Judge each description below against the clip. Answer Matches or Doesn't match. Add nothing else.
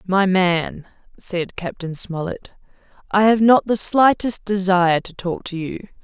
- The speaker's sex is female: Matches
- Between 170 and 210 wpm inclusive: Doesn't match